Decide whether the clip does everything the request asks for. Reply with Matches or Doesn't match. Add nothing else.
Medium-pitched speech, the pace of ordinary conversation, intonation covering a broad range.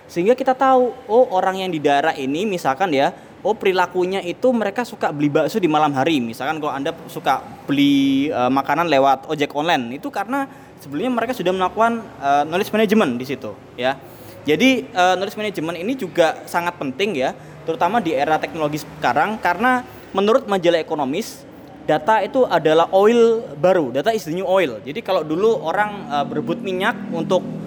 Doesn't match